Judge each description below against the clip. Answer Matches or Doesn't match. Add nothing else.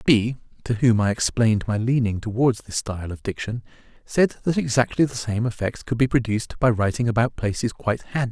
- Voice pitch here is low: Matches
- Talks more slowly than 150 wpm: Doesn't match